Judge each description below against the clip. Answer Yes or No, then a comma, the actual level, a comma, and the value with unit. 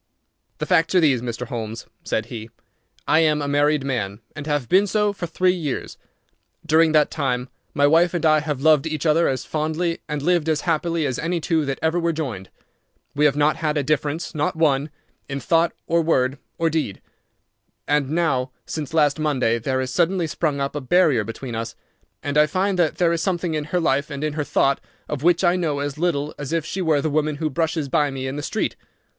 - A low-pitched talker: No, medium, 150 Hz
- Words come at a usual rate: No, fast, 215 wpm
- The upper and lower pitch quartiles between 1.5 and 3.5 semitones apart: Yes, average, 3.0 semitones